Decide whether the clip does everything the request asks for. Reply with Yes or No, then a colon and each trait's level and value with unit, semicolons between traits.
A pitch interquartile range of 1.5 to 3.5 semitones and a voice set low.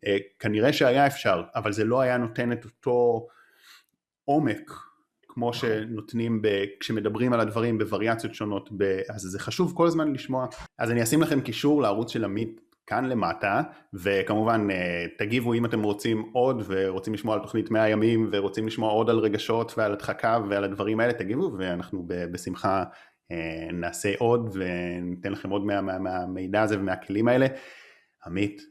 Yes: average, 2.9 semitones; low, 110 Hz